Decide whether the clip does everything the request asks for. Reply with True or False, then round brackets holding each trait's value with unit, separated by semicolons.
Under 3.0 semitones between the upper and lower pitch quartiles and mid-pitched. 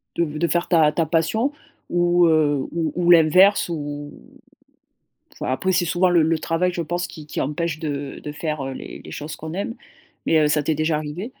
True (2.6 semitones; 160 Hz)